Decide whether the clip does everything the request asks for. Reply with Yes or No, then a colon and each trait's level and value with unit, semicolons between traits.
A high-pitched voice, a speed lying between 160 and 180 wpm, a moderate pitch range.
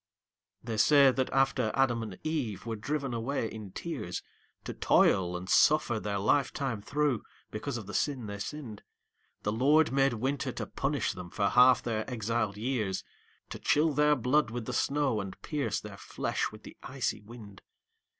No: low, 120 Hz; average, 175 wpm; average, 4.6 semitones